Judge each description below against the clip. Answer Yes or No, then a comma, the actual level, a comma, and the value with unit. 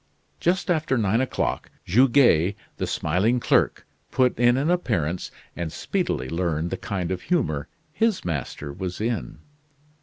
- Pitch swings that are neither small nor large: No, wide, 7.6 semitones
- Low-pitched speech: Yes, low, 105 Hz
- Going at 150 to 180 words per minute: No, average, 140 wpm